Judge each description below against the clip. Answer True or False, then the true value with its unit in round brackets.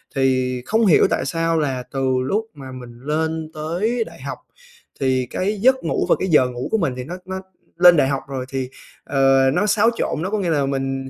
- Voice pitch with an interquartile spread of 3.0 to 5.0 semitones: False (5.5 semitones)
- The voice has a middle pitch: True (150 Hz)